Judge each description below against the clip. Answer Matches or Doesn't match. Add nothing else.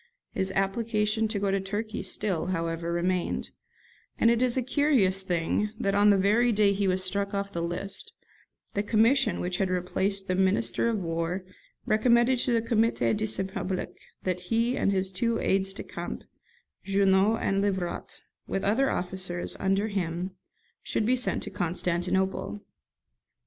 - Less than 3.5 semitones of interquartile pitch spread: Matches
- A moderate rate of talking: Matches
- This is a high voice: Matches